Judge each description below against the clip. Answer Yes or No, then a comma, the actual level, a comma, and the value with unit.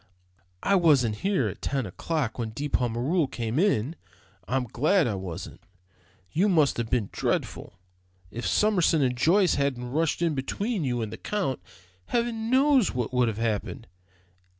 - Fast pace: No, average, 155 wpm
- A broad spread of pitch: Yes, wide, 7.5 semitones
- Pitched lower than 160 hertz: Yes, medium, 140 Hz